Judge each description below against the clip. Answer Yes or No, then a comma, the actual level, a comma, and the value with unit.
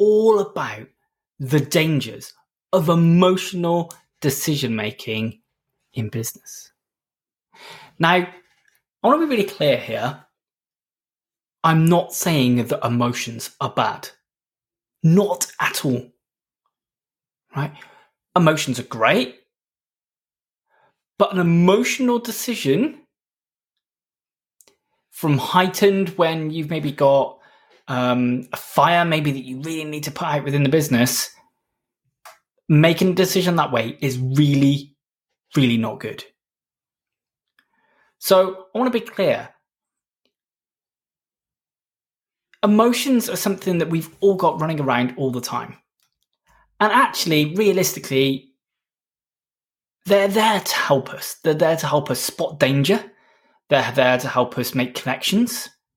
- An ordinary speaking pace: No, slow, 115 wpm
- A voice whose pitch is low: No, medium, 160 Hz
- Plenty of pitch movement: Yes, wide, 5.8 semitones